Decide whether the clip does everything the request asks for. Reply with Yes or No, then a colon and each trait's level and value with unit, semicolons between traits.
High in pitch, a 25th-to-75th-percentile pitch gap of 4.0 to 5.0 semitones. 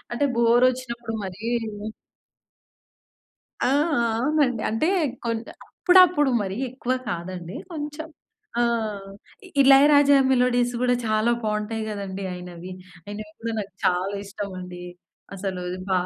Yes: high, 225 Hz; average, 4.7 semitones